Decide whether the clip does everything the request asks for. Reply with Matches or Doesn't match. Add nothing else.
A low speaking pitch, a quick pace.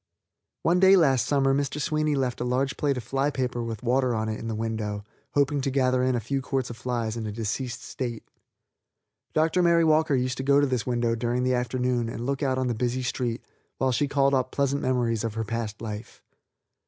Matches